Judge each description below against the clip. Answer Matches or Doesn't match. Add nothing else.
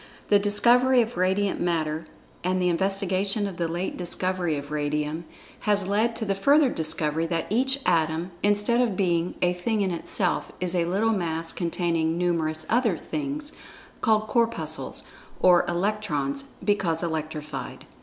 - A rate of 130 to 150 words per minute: Matches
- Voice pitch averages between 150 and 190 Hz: Matches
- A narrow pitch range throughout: Doesn't match